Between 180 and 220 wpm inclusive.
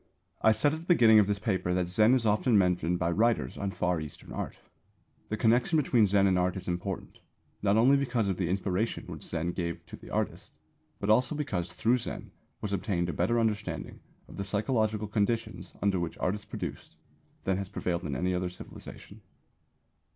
Yes: average, 195 wpm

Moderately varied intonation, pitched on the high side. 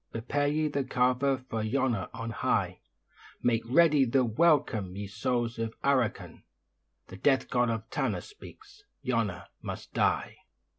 No: average, 3.6 semitones; low, 125 Hz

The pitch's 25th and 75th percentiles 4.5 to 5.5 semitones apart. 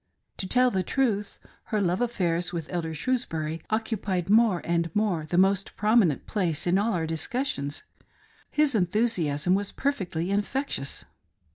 Yes: average, 4.8 semitones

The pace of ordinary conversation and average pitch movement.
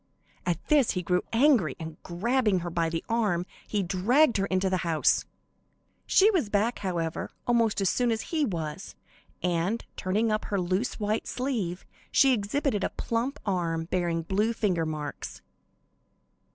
Yes: average, 155 wpm; average, 5.0 semitones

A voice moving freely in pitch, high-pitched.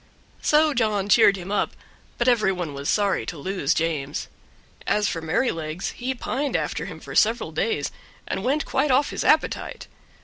Yes: wide, 6.9 semitones; high, 200 Hz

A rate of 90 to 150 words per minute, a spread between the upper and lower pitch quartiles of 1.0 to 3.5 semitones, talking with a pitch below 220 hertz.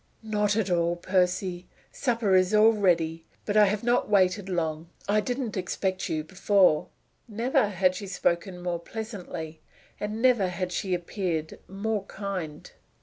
Yes: average, 145 wpm; average, 3.1 semitones; high, 190 Hz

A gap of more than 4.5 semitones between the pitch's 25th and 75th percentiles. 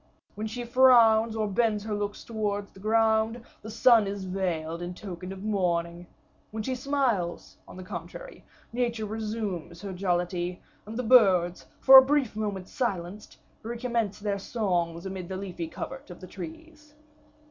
No: average, 4.1 semitones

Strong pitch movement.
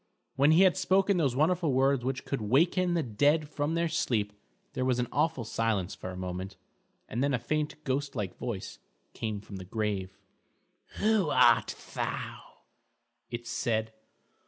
Yes: wide, 6.1 semitones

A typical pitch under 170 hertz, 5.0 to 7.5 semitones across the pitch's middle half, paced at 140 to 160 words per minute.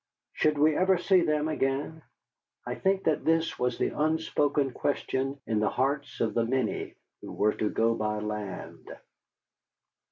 Yes: medium, 140 Hz; wide, 5.4 semitones; average, 155 wpm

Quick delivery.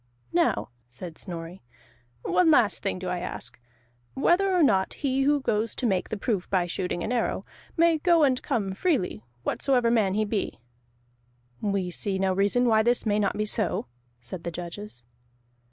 No: average, 170 wpm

